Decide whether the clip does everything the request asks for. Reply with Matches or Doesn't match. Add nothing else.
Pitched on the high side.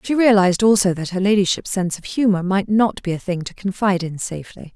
Matches